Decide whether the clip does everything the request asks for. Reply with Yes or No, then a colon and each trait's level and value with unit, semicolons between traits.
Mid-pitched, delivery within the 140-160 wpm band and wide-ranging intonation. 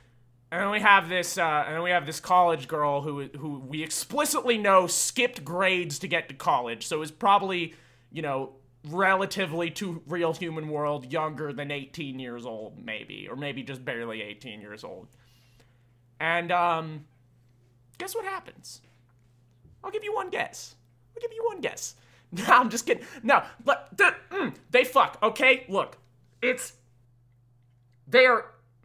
Yes: medium, 155 Hz; average, 155 wpm; wide, 7.7 semitones